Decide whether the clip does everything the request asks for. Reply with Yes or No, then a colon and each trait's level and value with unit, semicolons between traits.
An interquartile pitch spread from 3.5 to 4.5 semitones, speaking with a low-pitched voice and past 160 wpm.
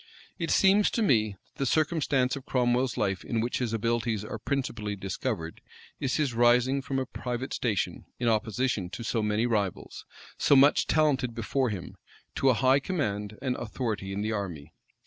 Yes: average, 4.0 semitones; low, 120 Hz; average, 175 wpm